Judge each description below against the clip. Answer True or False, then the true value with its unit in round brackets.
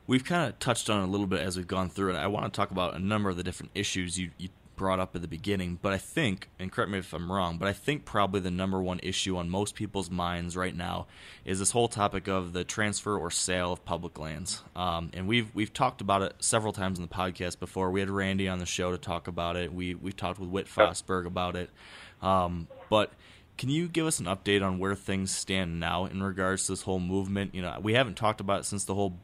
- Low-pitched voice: True (95 Hz)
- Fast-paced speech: True (260 wpm)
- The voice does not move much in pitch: True (1.9 semitones)